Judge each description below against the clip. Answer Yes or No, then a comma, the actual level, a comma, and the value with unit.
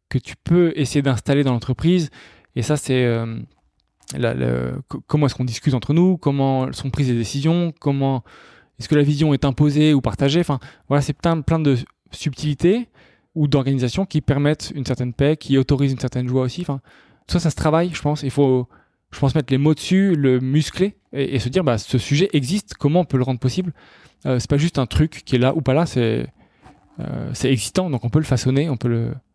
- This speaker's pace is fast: Yes, fast, 225 wpm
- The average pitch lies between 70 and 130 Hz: No, medium, 140 Hz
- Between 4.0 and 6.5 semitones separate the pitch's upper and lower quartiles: No, average, 3.2 semitones